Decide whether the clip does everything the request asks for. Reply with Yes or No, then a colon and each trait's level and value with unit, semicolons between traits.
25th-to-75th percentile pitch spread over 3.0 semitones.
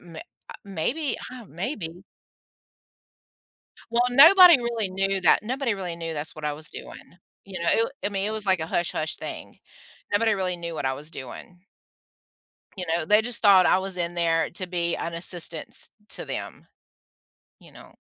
Yes: average, 4.2 semitones